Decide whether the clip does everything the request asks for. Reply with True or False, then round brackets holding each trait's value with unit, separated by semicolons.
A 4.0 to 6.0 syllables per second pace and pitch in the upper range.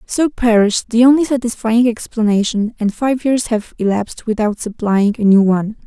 True (5.2 syllables/s; 225 Hz)